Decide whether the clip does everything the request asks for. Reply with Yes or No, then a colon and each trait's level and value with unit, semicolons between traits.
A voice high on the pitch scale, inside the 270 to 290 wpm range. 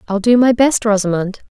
No: high, 215 Hz; average, 200 wpm